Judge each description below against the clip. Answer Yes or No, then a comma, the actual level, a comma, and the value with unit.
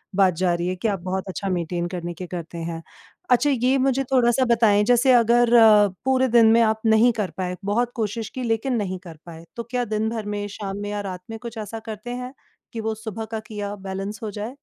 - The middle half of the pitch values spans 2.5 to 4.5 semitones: Yes, average, 3.8 semitones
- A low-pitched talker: No, high, 215 Hz